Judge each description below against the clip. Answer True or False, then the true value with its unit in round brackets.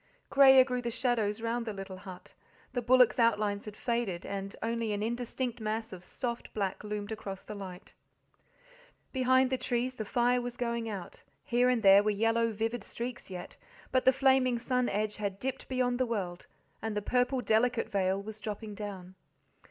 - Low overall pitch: False (225 Hz)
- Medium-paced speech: True (180 wpm)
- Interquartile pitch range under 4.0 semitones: True (3.2 semitones)